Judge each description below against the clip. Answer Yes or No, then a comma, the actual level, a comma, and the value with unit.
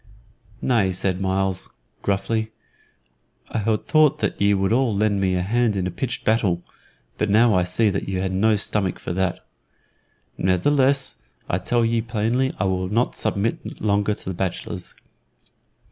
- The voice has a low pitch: Yes, low, 100 Hz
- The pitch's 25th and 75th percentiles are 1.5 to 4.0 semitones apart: Yes, average, 3.3 semitones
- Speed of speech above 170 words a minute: No, average, 160 wpm